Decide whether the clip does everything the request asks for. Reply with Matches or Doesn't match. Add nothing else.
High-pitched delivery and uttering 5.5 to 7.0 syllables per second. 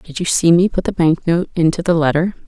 Doesn't match